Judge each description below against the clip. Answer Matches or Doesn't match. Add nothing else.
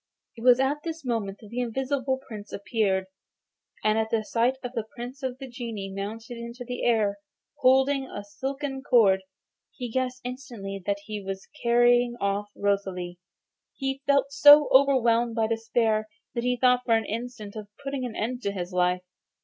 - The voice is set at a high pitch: Matches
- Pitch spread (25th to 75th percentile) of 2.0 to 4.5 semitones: Matches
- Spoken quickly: Doesn't match